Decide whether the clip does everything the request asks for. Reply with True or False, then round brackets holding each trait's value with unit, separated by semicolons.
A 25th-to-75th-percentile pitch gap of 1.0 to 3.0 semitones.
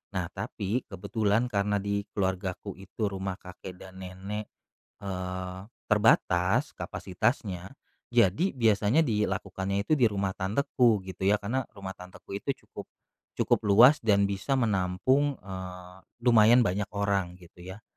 True (2.7 semitones)